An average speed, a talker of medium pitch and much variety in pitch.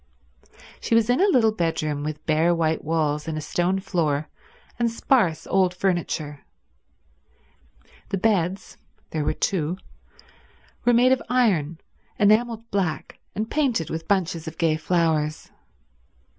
No: slow, 125 wpm; medium, 175 Hz; wide, 5.7 semitones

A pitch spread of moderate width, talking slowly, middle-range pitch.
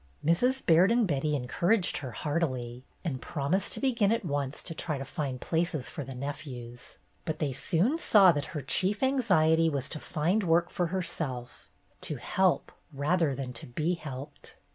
No: average, 4.9 semitones; average, 170 wpm; medium, 155 Hz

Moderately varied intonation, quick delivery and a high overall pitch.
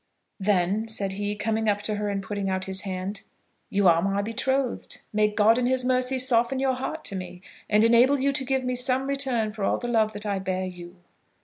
Yes: average, 4.4 semitones; fast, 220 wpm; high, 215 Hz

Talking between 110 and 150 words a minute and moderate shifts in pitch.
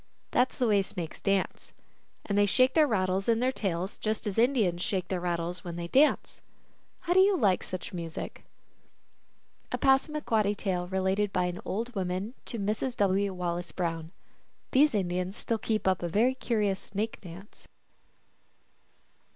No: average, 160 wpm; average, 4.2 semitones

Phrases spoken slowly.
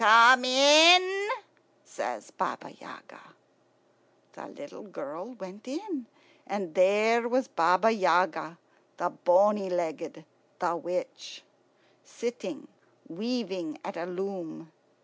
Yes: slow, 100 wpm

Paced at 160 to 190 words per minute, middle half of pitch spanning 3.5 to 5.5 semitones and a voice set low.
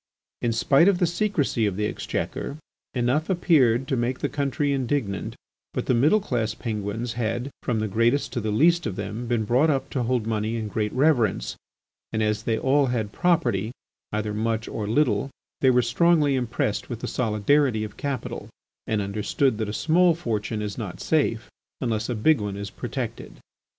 Yes: average, 180 wpm; average, 4.6 semitones; low, 120 Hz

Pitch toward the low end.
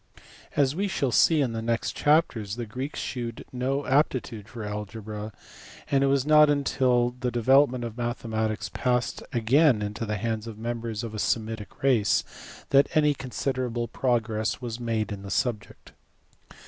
Yes: low, 120 Hz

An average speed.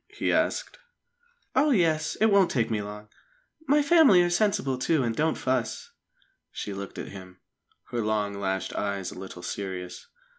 Yes: average, 160 wpm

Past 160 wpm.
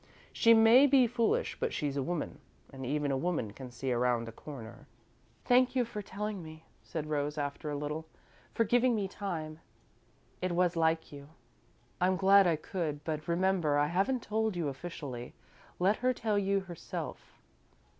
Yes: average, 170 wpm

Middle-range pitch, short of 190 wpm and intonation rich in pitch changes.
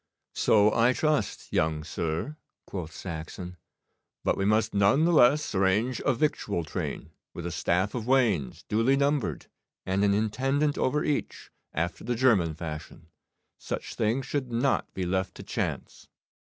No: low, 105 Hz; average, 150 wpm; wide, 6.9 semitones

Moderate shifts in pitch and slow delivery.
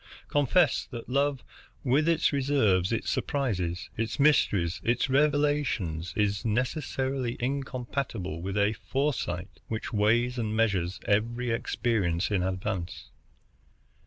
No: wide, 5.7 semitones; slow, 110 wpm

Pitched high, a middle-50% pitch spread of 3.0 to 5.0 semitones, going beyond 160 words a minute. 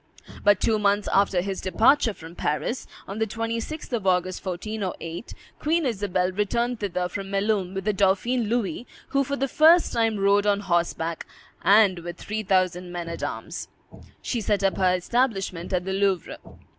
Yes: high, 200 Hz; average, 3.6 semitones; average, 170 wpm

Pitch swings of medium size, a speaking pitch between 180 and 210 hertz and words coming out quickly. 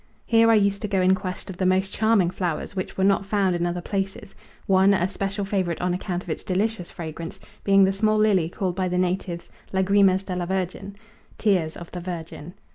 No: narrow, 1.9 semitones; high, 190 Hz; fast, 210 wpm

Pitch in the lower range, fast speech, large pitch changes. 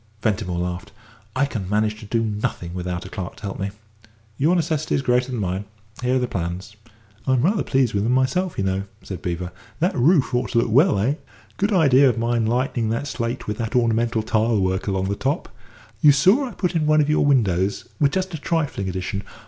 Yes: low, 115 Hz; fast, 215 wpm; wide, 6.1 semitones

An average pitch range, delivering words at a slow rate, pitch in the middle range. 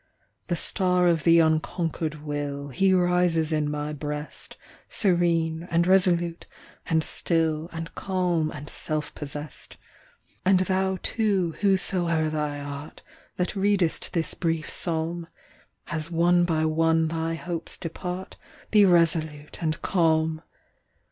No: narrow, 2.2 semitones; slow, 120 wpm; medium, 165 Hz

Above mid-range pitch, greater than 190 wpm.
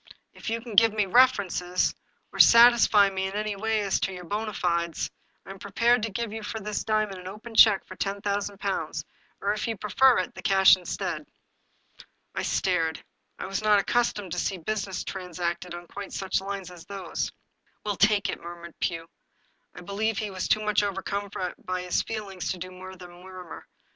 Yes: high, 195 Hz; average, 200 wpm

